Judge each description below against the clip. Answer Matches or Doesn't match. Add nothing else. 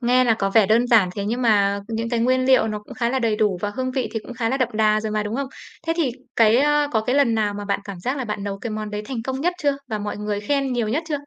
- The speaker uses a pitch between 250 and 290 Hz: Doesn't match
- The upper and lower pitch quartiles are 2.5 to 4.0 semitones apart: Matches